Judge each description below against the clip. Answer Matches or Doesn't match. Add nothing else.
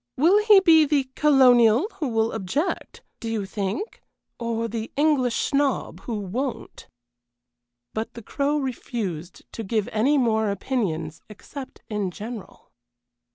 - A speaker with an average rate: Doesn't match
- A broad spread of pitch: Doesn't match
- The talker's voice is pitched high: Matches